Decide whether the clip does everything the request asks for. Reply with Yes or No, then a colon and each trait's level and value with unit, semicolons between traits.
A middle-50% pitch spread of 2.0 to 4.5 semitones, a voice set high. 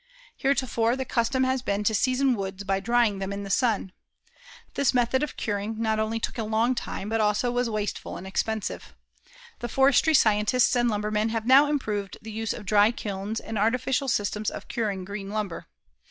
Yes: average, 3.0 semitones; high, 220 Hz